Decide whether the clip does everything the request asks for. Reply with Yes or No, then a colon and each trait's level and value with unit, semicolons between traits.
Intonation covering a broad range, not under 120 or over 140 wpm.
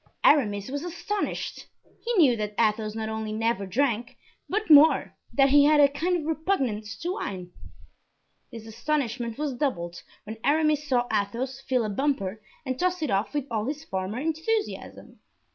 No: wide, 5.7 semitones; average, 160 wpm